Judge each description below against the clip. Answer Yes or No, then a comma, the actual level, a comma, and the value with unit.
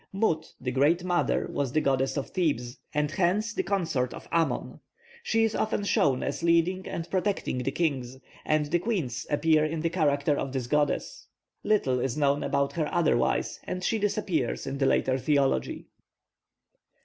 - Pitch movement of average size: Yes, average, 4.6 semitones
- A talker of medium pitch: Yes, medium, 155 Hz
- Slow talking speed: No, average, 170 wpm